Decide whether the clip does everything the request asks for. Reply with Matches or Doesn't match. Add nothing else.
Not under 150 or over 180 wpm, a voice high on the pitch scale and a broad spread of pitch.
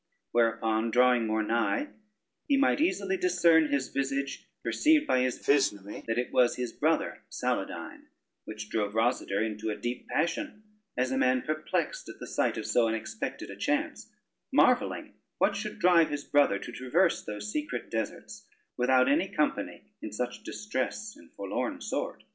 Doesn't match